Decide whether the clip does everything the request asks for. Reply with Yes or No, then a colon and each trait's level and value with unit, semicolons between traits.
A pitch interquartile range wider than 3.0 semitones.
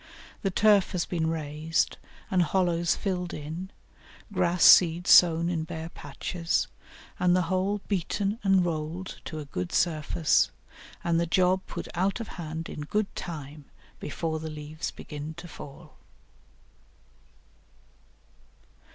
No: average, 2.7 semitones